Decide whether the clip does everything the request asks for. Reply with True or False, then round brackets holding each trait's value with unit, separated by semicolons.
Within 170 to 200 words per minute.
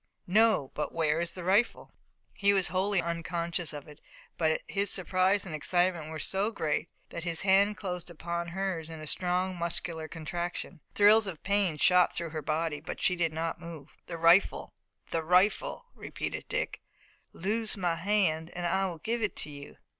True (175 wpm)